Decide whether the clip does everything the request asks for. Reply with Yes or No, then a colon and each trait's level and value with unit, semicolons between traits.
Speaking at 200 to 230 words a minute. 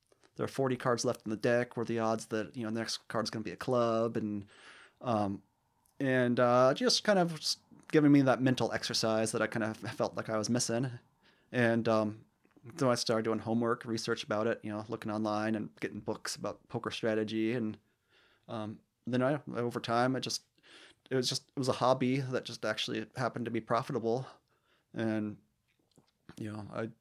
Yes: fast, 205 wpm